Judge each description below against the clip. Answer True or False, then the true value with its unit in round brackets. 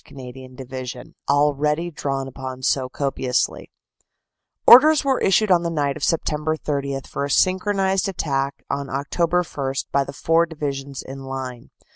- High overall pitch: False (140 Hz)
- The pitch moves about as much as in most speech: True (3.8 semitones)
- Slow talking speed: False (145 wpm)